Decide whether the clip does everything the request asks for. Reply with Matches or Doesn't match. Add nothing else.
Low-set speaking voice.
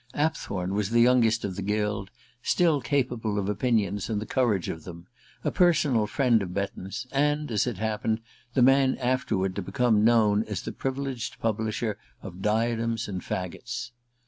Matches